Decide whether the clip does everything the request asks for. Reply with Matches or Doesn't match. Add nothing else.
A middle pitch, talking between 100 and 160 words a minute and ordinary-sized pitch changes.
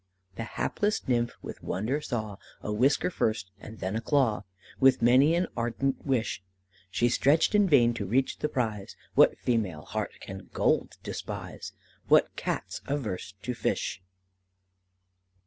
Doesn't match